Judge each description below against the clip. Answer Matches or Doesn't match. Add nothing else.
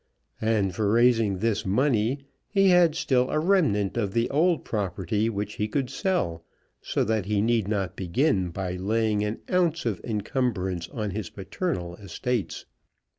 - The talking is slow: Doesn't match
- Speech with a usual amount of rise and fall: Matches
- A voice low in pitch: Matches